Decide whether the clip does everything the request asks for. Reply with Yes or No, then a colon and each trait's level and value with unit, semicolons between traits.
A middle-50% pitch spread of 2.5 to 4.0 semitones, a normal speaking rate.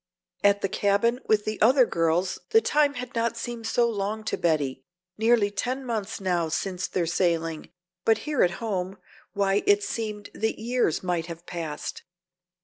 No: average, 4.6 semitones; average, 165 wpm